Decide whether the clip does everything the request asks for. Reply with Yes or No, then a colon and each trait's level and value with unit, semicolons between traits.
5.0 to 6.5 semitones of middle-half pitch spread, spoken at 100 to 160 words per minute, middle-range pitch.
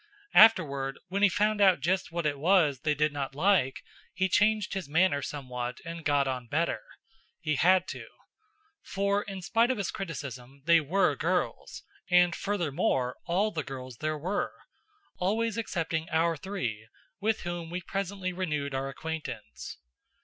Yes: wide, 5.4 semitones; average, 155 wpm; medium, 170 Hz